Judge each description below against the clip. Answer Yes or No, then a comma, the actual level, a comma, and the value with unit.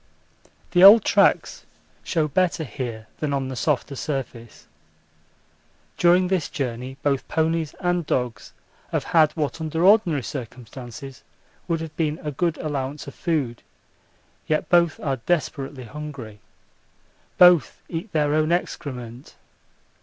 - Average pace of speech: No, slow, 125 wpm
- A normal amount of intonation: Yes, average, 4.1 semitones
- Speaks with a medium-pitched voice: Yes, medium, 150 Hz